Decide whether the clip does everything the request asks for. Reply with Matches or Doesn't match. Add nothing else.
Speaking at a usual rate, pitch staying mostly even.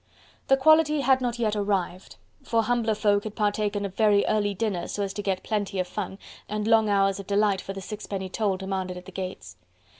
Doesn't match